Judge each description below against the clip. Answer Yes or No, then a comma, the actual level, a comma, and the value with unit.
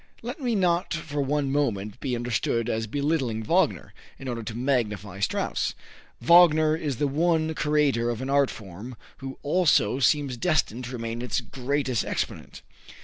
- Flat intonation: No, average, 4.6 semitones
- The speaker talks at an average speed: Yes, average, 155 wpm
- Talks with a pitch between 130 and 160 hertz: Yes, low, 135 Hz